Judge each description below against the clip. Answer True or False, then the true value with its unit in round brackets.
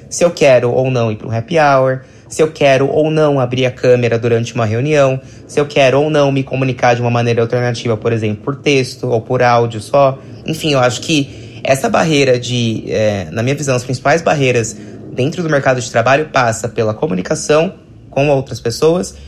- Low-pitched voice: True (125 Hz)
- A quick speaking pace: True (205 wpm)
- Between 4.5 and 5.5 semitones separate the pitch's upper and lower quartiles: False (3.3 semitones)